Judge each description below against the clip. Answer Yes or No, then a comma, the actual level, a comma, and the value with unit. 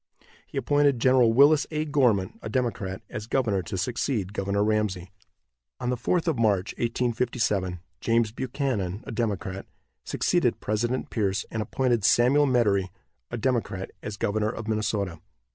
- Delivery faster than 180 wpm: No, average, 145 wpm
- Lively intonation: No, average, 4.0 semitones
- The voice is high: No, low, 110 Hz